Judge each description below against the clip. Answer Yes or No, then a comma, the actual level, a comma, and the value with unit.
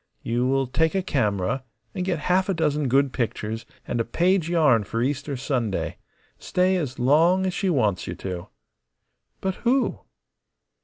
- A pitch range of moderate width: No, wide, 7.0 semitones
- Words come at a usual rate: Yes, average, 160 wpm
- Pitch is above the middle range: No, medium, 140 Hz